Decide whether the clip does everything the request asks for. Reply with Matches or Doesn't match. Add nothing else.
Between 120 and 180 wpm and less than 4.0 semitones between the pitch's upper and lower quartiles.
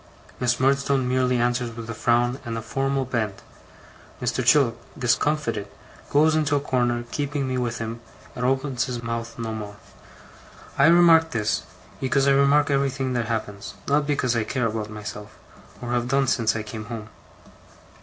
Matches